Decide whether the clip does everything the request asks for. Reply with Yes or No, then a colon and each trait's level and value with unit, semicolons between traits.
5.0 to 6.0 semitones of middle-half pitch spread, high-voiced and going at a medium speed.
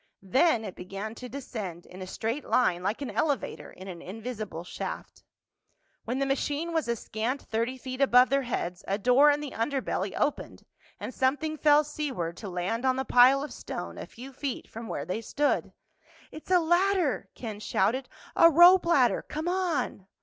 Yes: wide, 5.4 semitones; very high, 255 Hz; average, 180 wpm